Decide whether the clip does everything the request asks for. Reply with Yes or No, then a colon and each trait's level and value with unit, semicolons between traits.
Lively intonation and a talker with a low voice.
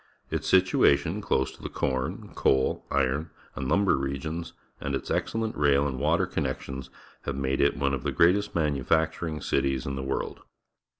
No: average, 3.7 semitones; very low, 70 Hz